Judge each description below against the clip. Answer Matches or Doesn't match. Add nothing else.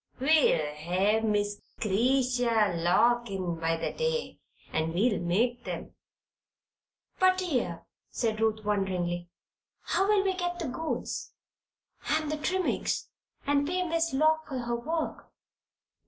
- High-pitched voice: Matches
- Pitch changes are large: Matches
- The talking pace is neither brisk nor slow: Doesn't match